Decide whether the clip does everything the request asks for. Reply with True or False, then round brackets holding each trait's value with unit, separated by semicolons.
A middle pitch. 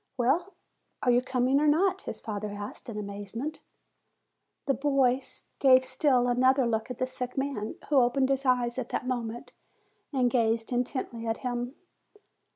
False (250 Hz)